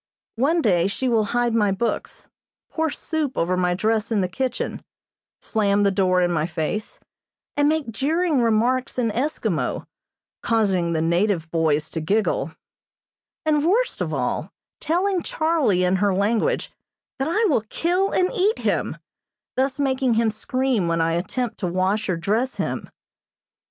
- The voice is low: No, high, 220 Hz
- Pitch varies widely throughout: Yes, wide, 7.0 semitones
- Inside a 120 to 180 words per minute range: Yes, average, 155 wpm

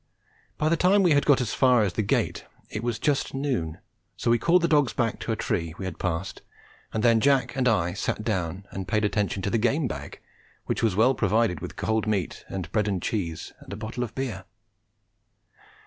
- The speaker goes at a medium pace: No, fast, 215 wpm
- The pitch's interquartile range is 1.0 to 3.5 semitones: No, average, 4.9 semitones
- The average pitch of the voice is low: Yes, low, 110 Hz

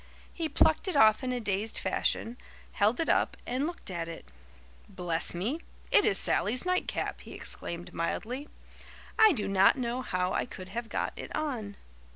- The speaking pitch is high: Yes, high, 225 Hz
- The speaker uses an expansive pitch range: Yes, wide, 6.5 semitones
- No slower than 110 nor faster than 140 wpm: No, average, 175 wpm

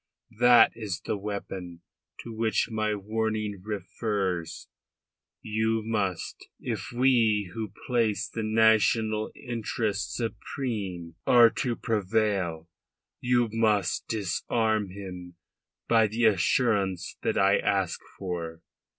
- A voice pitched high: No, low, 105 Hz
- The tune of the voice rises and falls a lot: No, average, 2.7 semitones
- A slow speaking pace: Yes, slow, 105 wpm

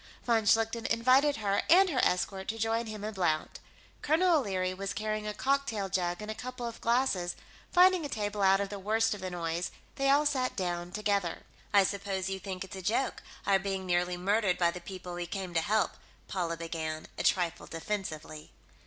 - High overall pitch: Yes, high, 200 Hz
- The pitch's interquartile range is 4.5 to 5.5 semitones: No, average, 3.8 semitones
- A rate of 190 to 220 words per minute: Yes, average, 195 wpm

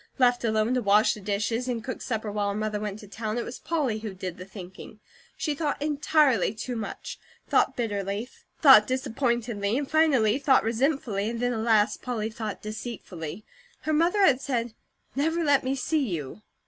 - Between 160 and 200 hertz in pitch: No, high, 230 Hz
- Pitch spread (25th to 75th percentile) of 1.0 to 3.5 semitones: No, average, 4.2 semitones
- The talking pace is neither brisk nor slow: Yes, average, 180 wpm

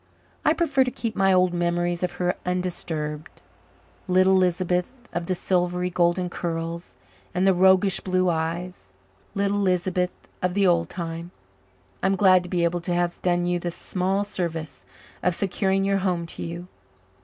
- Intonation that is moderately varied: No, narrow, 1.6 semitones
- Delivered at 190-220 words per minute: No, average, 160 wpm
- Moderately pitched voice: Yes, medium, 180 Hz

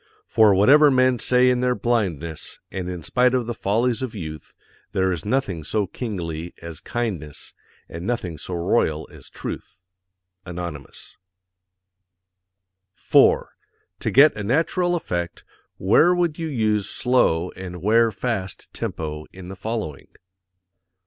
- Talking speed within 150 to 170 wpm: No, slow, 135 wpm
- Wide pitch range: Yes, wide, 6.2 semitones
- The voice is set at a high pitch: No, low, 105 Hz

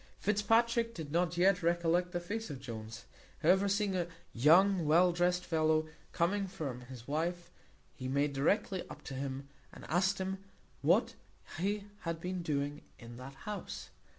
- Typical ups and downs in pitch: Yes, average, 5.0 semitones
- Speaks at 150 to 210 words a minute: Yes, average, 155 wpm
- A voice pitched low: No, medium, 175 Hz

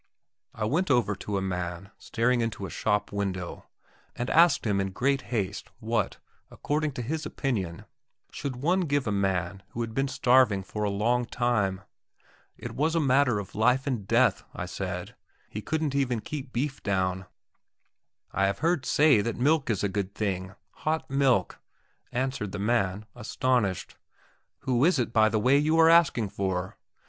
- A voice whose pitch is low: Yes, low, 115 Hz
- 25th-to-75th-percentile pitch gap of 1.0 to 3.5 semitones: No, wide, 5.5 semitones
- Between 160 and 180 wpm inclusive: Yes, average, 170 wpm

